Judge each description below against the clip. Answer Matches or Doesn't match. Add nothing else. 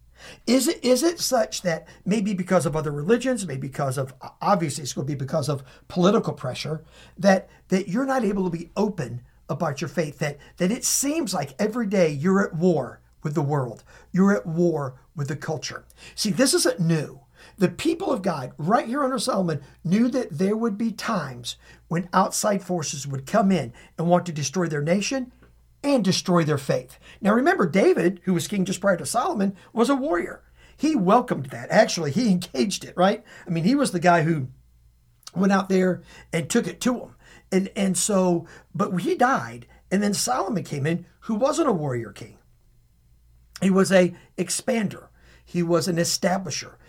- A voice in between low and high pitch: Matches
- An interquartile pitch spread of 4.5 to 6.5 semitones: Matches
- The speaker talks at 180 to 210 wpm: Matches